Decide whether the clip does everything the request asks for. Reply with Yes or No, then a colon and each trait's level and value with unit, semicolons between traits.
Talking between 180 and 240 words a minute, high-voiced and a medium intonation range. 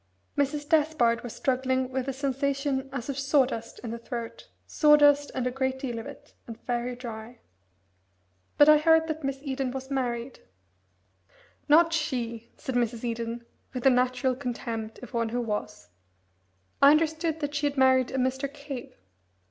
No: average, 165 wpm; very high, 260 Hz; average, 3.1 semitones